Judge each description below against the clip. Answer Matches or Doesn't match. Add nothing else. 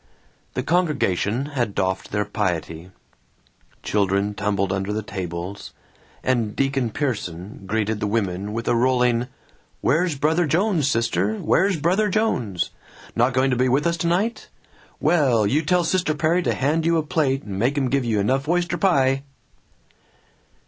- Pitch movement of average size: Doesn't match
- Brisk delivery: Doesn't match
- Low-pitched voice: Matches